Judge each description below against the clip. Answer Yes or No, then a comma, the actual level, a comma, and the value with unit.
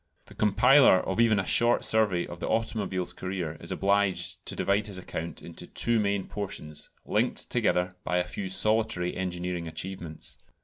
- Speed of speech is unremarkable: Yes, average, 165 wpm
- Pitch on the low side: Yes, very low, 95 Hz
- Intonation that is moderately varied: Yes, average, 3.2 semitones